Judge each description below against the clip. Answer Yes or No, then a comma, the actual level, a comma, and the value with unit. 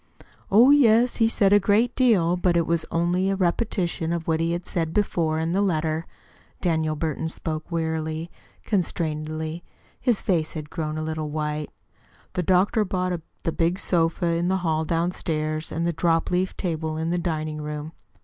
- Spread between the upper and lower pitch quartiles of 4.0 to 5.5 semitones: No, narrow, 2.6 semitones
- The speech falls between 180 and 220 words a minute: No, average, 170 wpm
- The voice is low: No, medium, 165 Hz